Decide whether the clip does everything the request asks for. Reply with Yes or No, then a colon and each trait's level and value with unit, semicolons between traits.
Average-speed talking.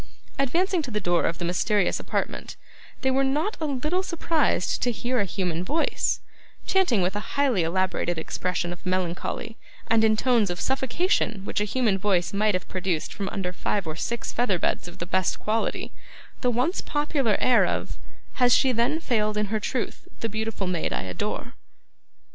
Yes: average, 180 wpm